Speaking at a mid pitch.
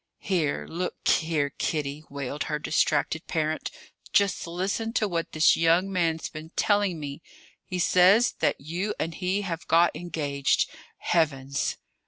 Yes: medium, 165 Hz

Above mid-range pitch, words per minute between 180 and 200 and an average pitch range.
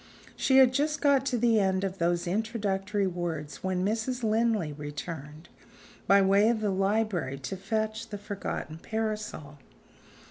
No: high, 200 Hz; average, 145 wpm; average, 4.3 semitones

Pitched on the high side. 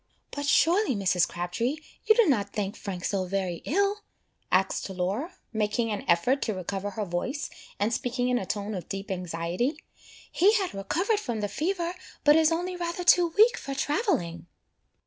Yes: high, 230 Hz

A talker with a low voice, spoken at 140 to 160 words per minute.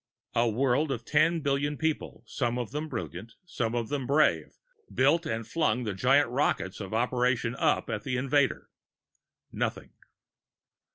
Yes: low, 125 Hz; average, 150 wpm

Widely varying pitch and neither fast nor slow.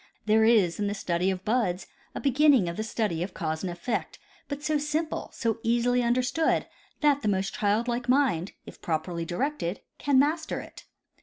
Yes: wide, 6.8 semitones; average, 175 wpm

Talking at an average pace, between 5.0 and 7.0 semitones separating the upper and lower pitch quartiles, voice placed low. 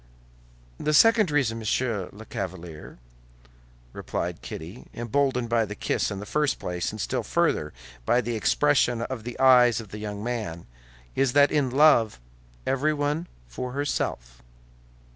Yes: average, 145 wpm; average, 5.3 semitones; low, 120 Hz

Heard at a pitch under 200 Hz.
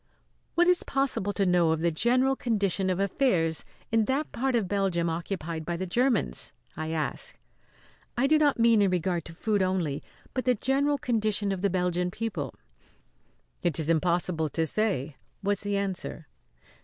Yes: high, 190 Hz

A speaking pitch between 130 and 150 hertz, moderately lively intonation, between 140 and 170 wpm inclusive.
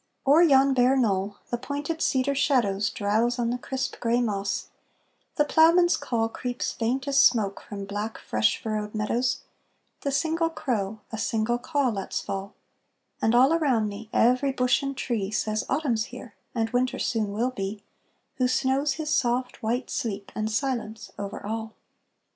No: high, 240 Hz; average, 3.9 semitones; average, 165 wpm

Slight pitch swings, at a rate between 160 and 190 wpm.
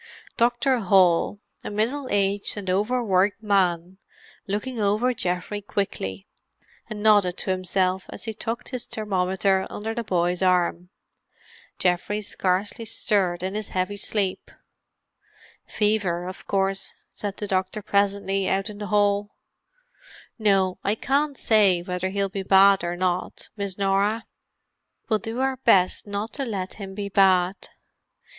No: narrow, 2.2 semitones; average, 140 wpm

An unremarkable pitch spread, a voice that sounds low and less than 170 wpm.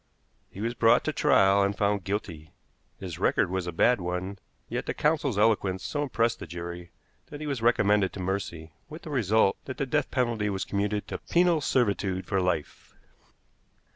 No: average, 4.4 semitones; low, 100 Hz; average, 180 wpm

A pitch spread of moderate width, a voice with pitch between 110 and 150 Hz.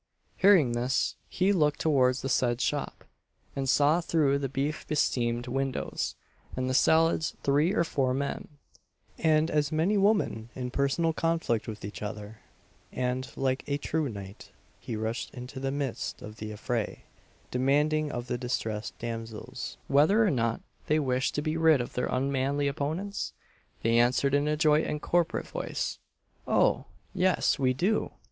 Yes: average, 4.0 semitones; low, 135 Hz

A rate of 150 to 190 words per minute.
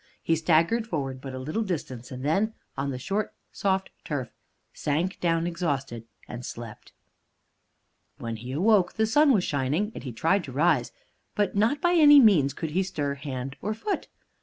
Yes: average, 175 wpm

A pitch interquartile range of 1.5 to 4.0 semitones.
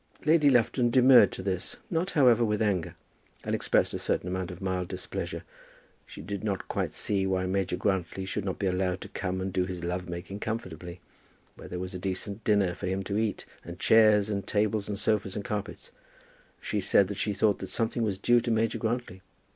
Yes: average, 2.8 semitones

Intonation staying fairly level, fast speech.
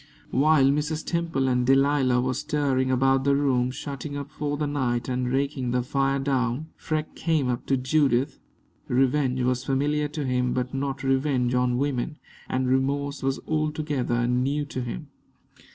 No: narrow, 2.3 semitones; average, 160 wpm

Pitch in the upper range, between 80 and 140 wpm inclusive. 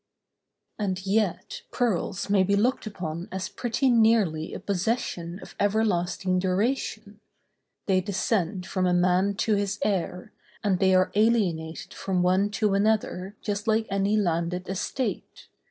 Yes: high, 195 Hz; slow, 135 wpm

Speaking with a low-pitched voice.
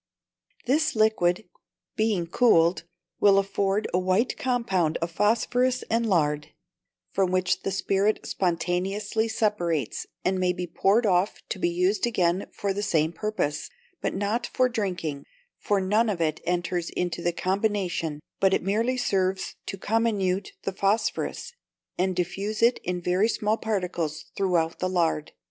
No: high, 190 Hz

